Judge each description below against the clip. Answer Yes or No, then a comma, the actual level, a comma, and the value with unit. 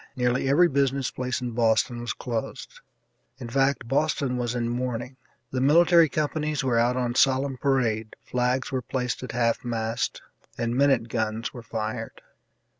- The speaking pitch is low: Yes, low, 125 Hz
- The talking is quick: No, average, 155 wpm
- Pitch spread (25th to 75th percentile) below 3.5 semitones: Yes, narrow, 2.4 semitones